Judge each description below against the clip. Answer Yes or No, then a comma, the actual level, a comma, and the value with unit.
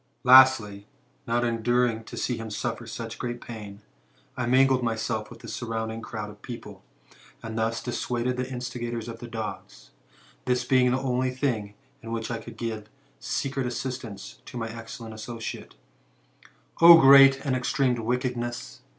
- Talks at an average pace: Yes, average, 155 wpm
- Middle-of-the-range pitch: No, low, 120 Hz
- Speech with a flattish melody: Yes, narrow, 2.1 semitones